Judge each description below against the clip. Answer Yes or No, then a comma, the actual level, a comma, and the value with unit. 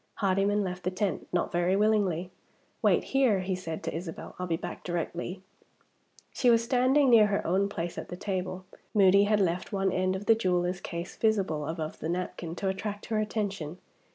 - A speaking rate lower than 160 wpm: No, average, 185 wpm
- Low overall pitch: No, high, 190 Hz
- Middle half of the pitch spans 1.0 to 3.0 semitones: Yes, average, 2.7 semitones